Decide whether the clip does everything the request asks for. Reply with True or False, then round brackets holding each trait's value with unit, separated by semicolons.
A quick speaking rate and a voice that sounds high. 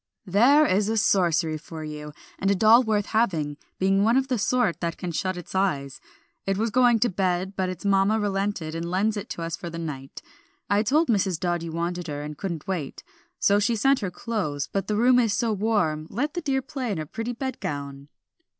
True (215 wpm; 195 Hz)